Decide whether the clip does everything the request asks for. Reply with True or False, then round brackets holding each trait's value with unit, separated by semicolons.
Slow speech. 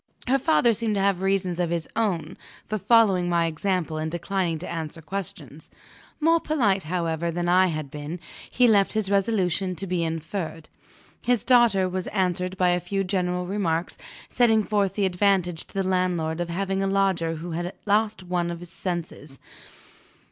False (170 wpm)